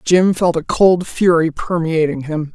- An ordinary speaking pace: Yes, average, 165 wpm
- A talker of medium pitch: Yes, medium, 165 Hz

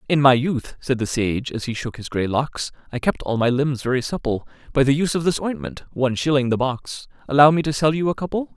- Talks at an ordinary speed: No, fast, 245 wpm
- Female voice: No, male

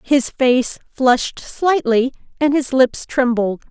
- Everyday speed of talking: No, slow, 130 wpm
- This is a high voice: Yes, very high, 260 Hz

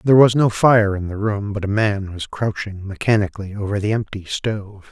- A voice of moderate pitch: No, low, 105 Hz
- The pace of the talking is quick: Yes, fast, 210 wpm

